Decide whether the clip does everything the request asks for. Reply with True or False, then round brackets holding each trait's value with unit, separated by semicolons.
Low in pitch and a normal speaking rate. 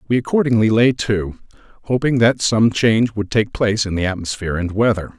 True (110 Hz; 185 wpm)